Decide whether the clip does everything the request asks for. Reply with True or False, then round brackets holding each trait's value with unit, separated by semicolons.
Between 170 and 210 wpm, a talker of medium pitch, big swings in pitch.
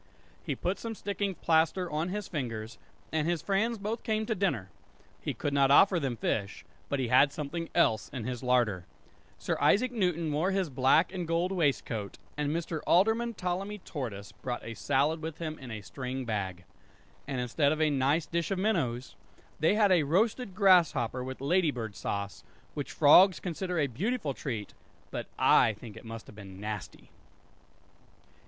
True (175 wpm; 150 Hz; 6.9 semitones)